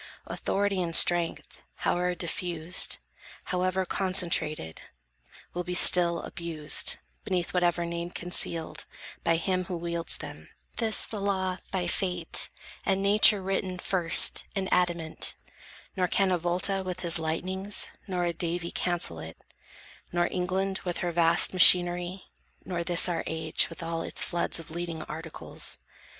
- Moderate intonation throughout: No, narrow, 1.7 semitones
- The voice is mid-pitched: Yes, medium, 175 Hz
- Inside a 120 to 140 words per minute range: Yes, slow, 135 wpm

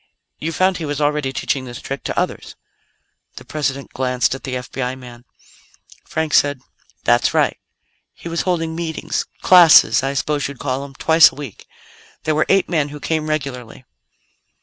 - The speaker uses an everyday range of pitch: Yes, average, 3.3 semitones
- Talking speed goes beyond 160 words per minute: Yes, average, 170 wpm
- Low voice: No, medium, 145 Hz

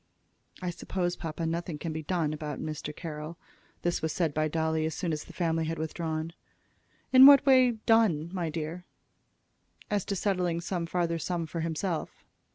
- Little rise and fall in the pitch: Yes, narrow, 2.3 semitones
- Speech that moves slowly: No, average, 170 wpm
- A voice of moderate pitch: Yes, medium, 165 Hz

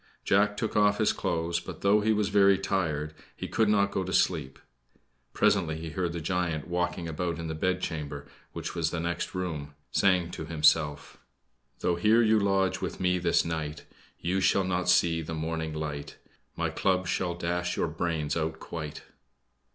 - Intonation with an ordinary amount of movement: Yes, average, 3.0 semitones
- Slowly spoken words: No, average, 175 wpm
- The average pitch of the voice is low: Yes, very low, 85 Hz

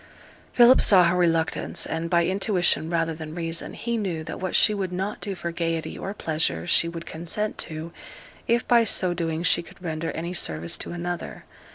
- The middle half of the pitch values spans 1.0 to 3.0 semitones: Yes, narrow, 2.5 semitones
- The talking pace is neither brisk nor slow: Yes, average, 190 wpm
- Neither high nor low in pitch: Yes, medium, 170 Hz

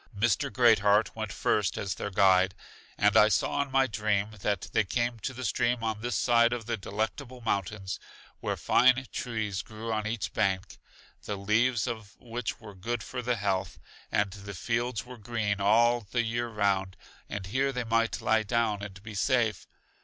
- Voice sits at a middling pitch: No, low, 110 Hz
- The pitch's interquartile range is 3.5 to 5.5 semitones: No, average, 2.8 semitones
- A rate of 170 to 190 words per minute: Yes, average, 185 wpm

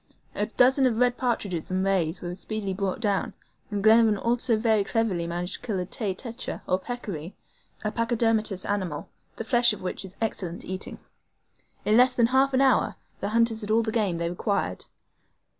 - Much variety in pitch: No, average, 3.7 semitones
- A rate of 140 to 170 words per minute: No, average, 185 wpm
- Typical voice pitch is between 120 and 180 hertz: No, high, 215 Hz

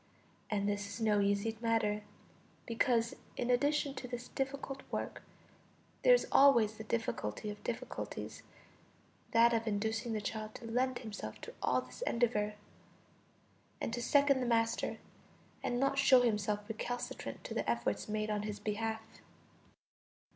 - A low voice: No, high, 230 Hz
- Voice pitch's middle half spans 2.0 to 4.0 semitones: Yes, average, 2.7 semitones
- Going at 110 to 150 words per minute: Yes, average, 145 wpm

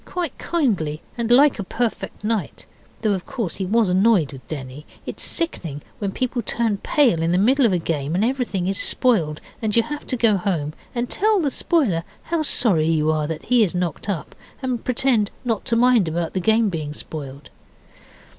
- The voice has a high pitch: Yes, high, 205 Hz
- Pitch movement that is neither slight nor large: No, wide, 6.9 semitones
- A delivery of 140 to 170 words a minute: No, average, 200 wpm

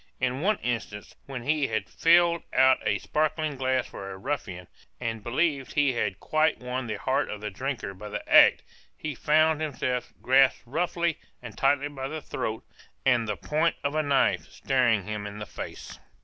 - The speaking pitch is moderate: No, low, 130 Hz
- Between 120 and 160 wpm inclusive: No, average, 180 wpm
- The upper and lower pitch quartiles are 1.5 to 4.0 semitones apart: No, average, 5.1 semitones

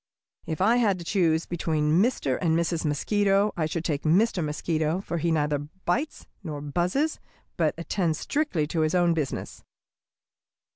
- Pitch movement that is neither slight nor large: Yes, average, 3.7 semitones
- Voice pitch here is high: No, medium, 170 Hz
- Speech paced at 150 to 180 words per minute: Yes, average, 155 wpm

